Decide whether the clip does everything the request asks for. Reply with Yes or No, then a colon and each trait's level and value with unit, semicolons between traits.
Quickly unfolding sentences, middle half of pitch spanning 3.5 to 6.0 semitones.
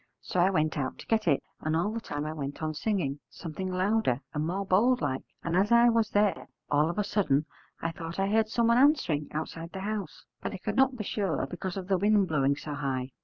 Yes: fast, 235 wpm; wide, 5.6 semitones